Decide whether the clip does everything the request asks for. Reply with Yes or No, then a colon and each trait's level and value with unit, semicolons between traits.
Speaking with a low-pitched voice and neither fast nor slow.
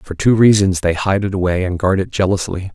No: very low, 95 Hz; fast, 240 wpm